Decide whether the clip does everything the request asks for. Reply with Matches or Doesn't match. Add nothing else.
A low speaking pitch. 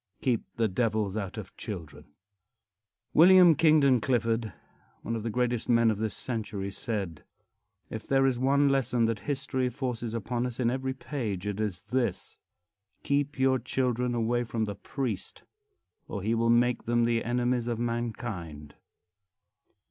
Matches